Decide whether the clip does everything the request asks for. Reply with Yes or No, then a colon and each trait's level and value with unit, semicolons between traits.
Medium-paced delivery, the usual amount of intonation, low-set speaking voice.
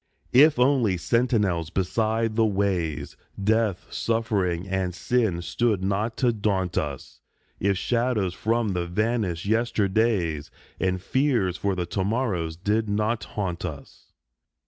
No: slow, 125 wpm; average, 4.1 semitones; low, 100 Hz